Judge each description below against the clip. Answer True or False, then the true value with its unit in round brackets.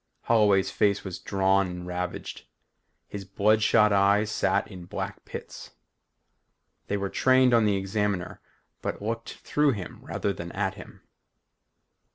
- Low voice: True (100 Hz)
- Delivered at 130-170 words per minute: True (135 wpm)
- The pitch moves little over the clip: True (2.0 semitones)